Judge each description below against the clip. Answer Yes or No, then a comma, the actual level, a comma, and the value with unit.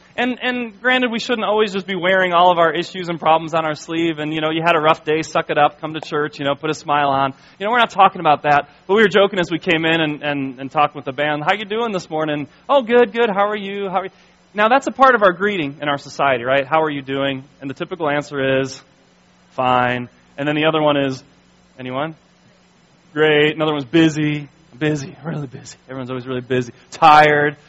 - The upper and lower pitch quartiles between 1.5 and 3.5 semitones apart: No, average, 4.5 semitones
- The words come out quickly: Yes, fast, 245 wpm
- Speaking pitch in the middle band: Yes, medium, 155 Hz